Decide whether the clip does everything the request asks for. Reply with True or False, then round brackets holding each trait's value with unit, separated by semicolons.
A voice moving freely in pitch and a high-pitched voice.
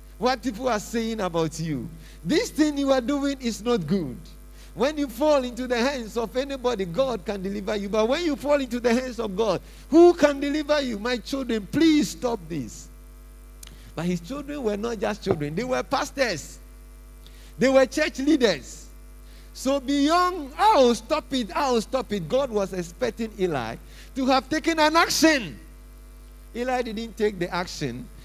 True (6.4 semitones; 240 Hz)